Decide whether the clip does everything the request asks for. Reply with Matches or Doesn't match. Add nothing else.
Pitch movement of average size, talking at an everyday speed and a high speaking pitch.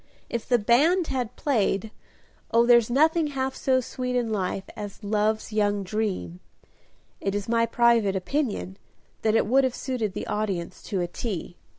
Matches